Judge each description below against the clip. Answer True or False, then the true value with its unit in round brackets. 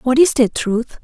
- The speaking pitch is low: False (255 Hz)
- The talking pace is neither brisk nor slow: False (230 wpm)